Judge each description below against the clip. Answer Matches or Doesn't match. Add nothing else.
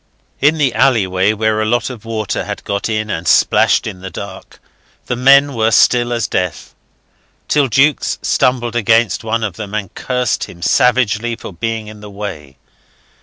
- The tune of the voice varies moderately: Matches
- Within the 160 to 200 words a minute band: Matches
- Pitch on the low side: Matches